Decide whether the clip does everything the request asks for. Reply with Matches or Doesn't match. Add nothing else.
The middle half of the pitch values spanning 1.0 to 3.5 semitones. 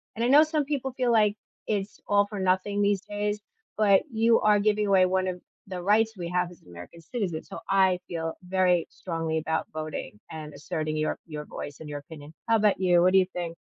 Doesn't match